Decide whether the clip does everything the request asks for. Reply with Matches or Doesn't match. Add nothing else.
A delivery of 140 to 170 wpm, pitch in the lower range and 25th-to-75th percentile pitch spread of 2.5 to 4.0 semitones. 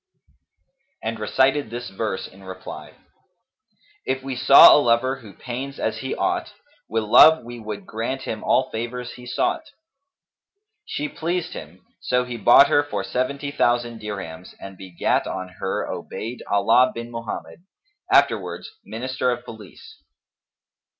Matches